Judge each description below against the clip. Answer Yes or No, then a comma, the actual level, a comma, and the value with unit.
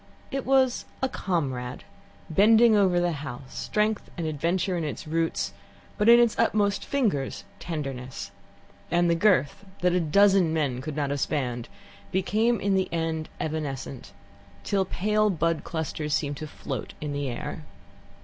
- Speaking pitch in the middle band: Yes, medium, 165 Hz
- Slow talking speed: No, average, 150 wpm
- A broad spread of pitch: Yes, wide, 5.7 semitones